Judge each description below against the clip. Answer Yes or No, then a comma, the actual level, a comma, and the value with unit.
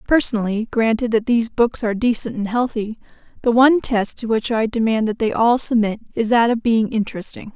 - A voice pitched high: Yes, high, 225 Hz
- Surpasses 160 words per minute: Yes, average, 200 wpm